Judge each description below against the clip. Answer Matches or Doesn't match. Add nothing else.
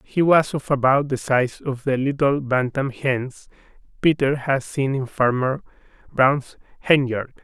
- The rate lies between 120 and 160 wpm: Matches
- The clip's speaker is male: Matches